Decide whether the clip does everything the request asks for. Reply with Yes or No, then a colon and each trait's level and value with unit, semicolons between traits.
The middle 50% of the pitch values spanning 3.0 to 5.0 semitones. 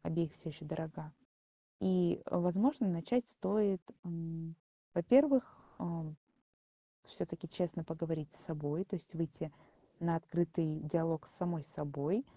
No: narrow, 2.6 semitones